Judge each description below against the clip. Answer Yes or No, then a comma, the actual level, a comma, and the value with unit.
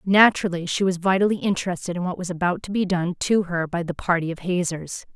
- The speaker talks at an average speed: No, fast, 220 wpm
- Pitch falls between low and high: Yes, medium, 180 Hz